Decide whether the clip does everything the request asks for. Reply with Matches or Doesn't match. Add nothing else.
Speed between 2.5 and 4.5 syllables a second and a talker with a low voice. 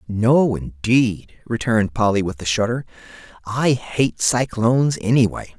Matches